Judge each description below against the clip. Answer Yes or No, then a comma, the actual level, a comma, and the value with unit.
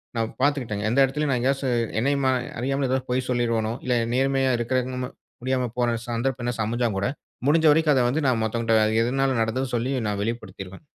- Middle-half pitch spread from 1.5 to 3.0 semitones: Yes, average, 2.7 semitones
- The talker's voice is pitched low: Yes, low, 125 Hz